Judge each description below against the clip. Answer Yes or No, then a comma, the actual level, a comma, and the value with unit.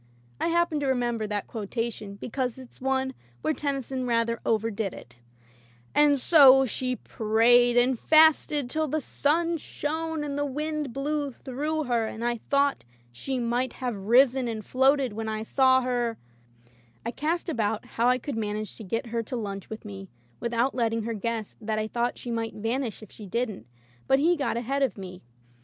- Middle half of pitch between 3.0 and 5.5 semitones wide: Yes, average, 3.9 semitones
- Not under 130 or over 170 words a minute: No, average, 185 wpm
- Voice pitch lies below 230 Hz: No, high, 245 Hz